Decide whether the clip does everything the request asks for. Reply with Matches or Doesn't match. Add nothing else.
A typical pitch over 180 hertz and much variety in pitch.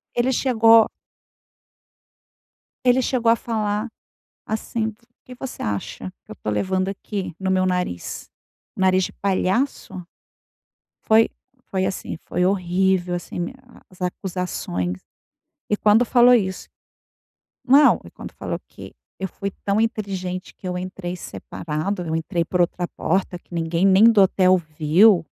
Doesn't match